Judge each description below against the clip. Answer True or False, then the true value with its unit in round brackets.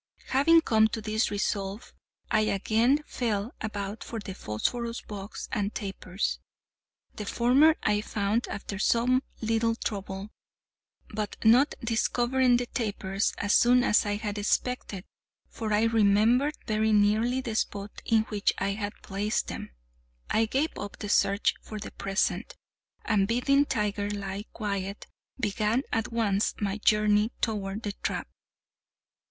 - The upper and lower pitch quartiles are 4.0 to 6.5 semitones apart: False (2.4 semitones)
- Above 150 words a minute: False (140 wpm)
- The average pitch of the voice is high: True (215 Hz)